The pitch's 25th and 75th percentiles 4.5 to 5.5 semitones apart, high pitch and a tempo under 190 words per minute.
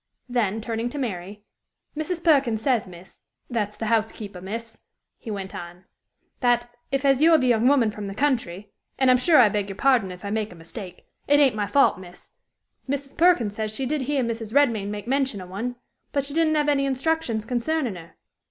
No: average, 5.0 semitones; high, 235 Hz; fast, 205 wpm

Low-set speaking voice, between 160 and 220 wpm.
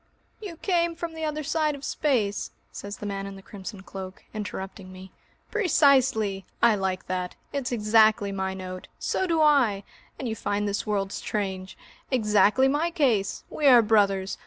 No: high, 210 Hz; average, 165 wpm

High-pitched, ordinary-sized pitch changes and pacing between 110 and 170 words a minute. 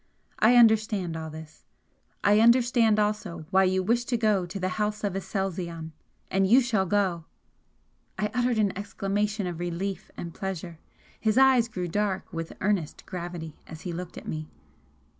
Yes: high, 195 Hz; average, 3.6 semitones; average, 165 wpm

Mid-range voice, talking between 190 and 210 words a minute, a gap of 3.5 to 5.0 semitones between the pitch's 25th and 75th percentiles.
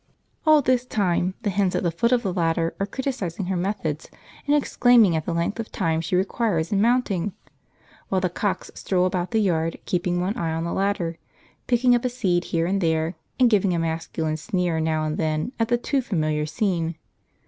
Yes: medium, 180 Hz; fast, 205 wpm; average, 4.7 semitones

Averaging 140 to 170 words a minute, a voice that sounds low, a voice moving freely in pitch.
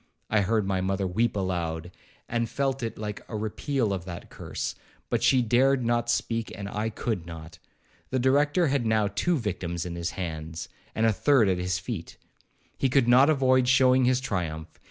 No: average, 185 wpm; low, 110 Hz; wide, 5.8 semitones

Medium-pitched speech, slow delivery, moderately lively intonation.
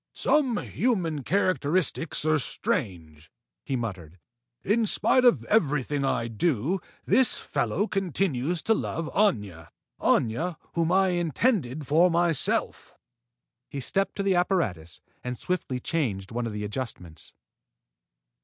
No: medium, 155 Hz; slow, 120 wpm; wide, 8.3 semitones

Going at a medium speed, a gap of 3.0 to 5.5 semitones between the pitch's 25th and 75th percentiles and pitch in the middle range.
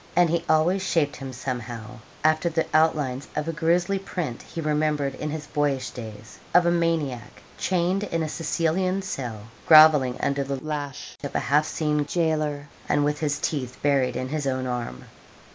Yes: average, 175 wpm; average, 3.7 semitones; medium, 150 Hz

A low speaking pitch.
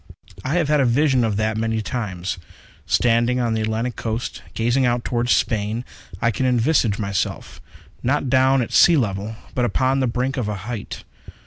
Yes: low, 120 Hz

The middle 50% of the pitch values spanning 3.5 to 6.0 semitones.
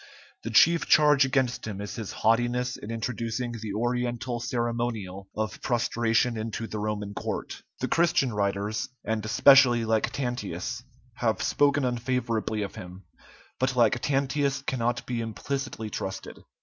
No: average, 2.7 semitones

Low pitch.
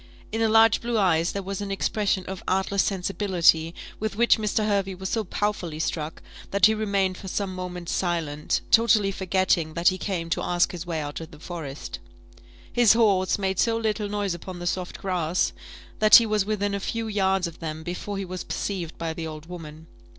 No: high, 190 Hz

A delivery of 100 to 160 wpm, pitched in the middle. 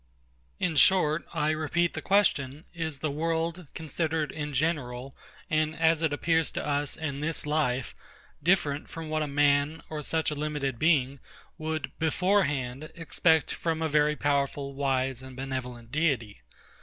Yes: average, 150 wpm; medium, 150 Hz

